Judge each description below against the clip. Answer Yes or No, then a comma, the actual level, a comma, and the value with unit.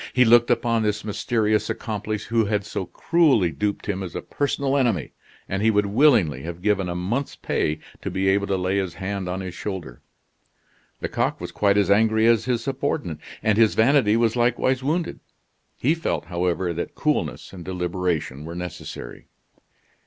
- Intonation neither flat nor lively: Yes, average, 4.3 semitones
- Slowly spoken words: No, average, 175 wpm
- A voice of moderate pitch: No, low, 105 Hz